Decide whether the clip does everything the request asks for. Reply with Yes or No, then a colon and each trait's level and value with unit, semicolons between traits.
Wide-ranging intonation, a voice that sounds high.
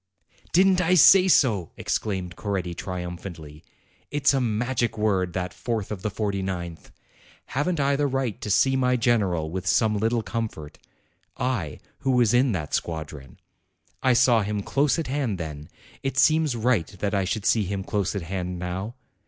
No: wide, 5.9 semitones; low, 105 Hz